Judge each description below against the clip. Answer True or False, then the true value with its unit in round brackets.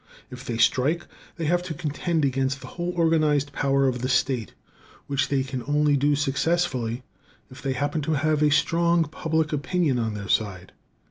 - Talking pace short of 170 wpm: False (180 wpm)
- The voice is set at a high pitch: False (145 Hz)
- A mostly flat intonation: False (3.3 semitones)